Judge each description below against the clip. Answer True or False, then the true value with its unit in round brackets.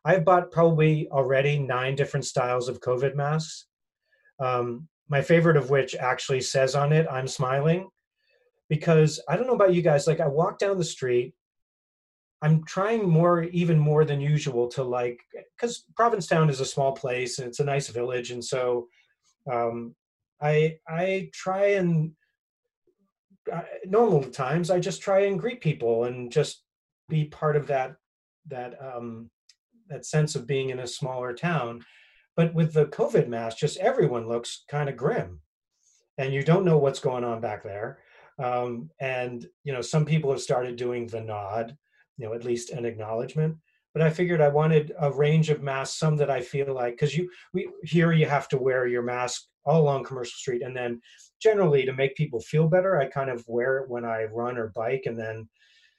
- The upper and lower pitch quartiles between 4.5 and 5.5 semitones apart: True (5.0 semitones)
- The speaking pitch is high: False (140 Hz)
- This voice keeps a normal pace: True (185 wpm)